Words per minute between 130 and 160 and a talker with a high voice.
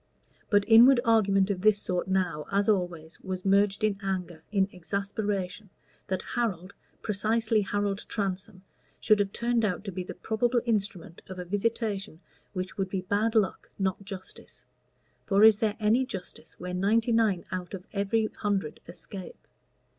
Yes: average, 155 wpm; high, 200 Hz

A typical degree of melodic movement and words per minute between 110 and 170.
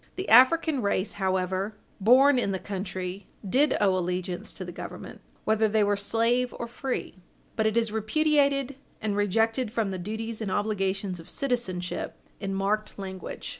Yes: average, 3.8 semitones; average, 160 wpm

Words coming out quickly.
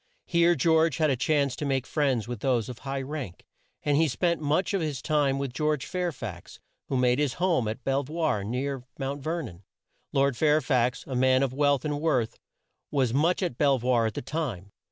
Yes: fast, 210 wpm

